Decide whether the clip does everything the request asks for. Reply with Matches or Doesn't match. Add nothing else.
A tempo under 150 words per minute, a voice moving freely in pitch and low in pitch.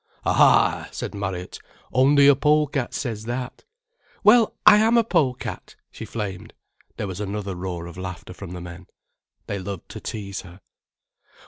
Doesn't match